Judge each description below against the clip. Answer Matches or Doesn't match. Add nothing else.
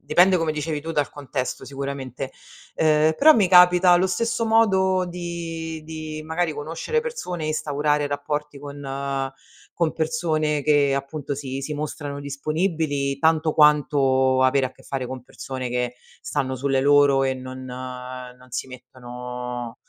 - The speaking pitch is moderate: Matches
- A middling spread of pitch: Matches